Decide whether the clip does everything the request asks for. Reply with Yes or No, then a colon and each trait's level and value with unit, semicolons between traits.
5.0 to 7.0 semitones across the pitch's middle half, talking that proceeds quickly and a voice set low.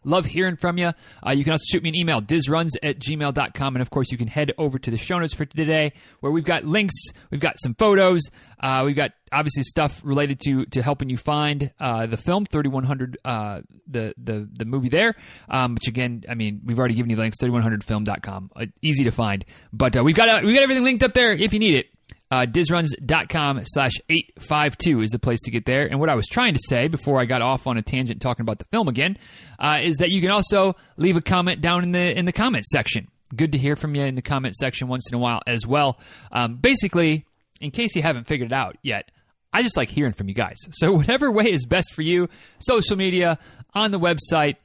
No: wide, 5.6 semitones; fast, 240 wpm; medium, 145 Hz